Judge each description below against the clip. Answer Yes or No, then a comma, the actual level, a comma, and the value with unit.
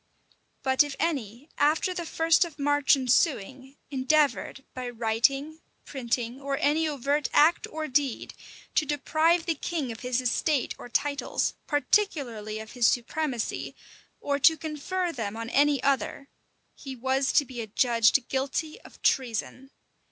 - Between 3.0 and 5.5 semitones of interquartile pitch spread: Yes, average, 3.7 semitones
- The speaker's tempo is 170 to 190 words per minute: No, average, 140 wpm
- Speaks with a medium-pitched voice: No, very high, 275 Hz